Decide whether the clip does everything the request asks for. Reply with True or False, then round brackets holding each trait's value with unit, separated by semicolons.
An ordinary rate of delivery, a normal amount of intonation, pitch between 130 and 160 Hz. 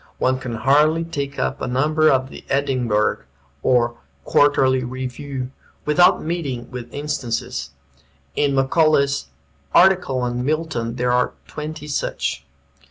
False (120 wpm; 3.3 semitones; 135 Hz)